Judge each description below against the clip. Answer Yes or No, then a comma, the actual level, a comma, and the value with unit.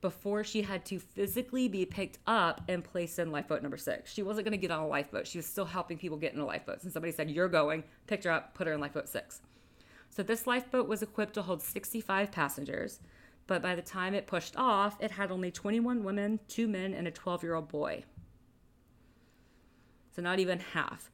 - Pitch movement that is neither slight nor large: Yes, average, 3.6 semitones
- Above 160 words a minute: Yes, fast, 205 wpm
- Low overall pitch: No, medium, 185 Hz